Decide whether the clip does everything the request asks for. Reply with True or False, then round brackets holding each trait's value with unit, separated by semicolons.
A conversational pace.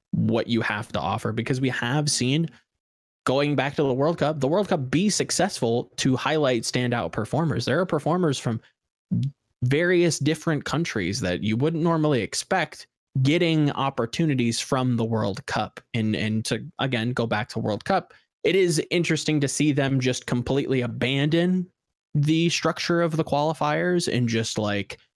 True (160 wpm)